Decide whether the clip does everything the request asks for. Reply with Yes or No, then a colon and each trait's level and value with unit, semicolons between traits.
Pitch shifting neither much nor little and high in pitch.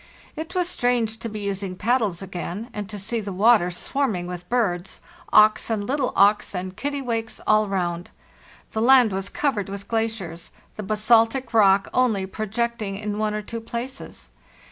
Yes: average, 3.2 semitones; high, 215 Hz